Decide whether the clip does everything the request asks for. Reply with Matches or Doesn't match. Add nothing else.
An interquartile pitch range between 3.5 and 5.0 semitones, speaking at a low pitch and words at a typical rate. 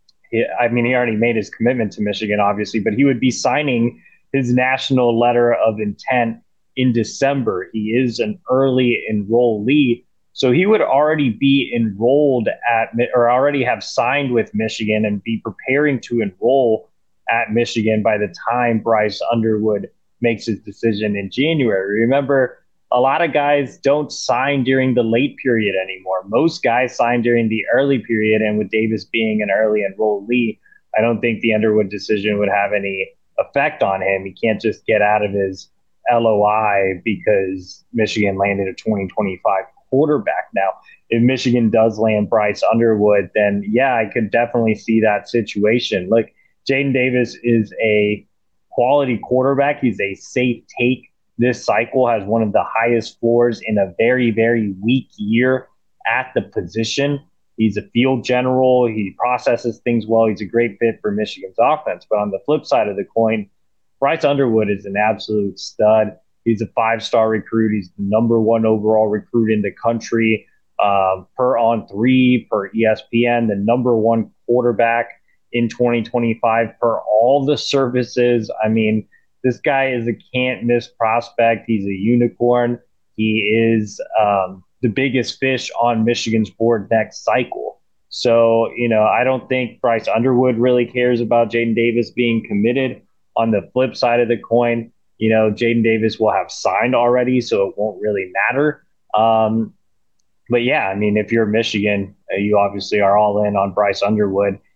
Doesn't match